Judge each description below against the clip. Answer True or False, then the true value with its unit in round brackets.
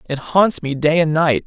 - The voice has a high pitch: False (155 Hz)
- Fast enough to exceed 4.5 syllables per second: False (4.4 syllables/s)